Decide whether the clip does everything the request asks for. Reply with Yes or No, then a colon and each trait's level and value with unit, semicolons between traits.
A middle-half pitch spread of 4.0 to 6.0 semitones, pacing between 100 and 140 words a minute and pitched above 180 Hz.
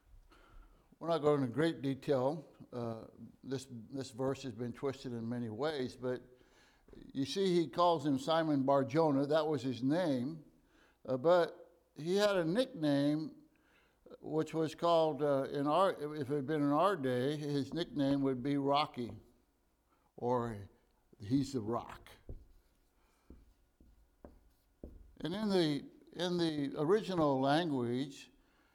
No: average, 4.3 semitones; slow, 135 wpm; medium, 140 Hz